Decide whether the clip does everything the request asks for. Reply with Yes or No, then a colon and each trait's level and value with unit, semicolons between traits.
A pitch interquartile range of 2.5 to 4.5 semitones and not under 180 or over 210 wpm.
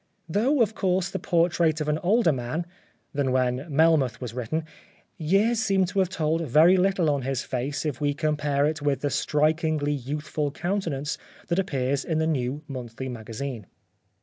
No: average, 4.1 semitones; average, 170 wpm